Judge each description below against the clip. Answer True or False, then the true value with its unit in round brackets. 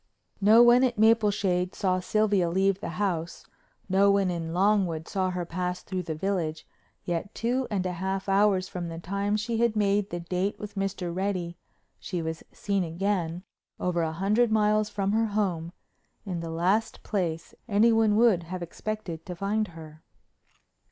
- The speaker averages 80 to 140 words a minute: False (165 wpm)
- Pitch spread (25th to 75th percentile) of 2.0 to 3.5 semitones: True (3.2 semitones)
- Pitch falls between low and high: False (195 Hz)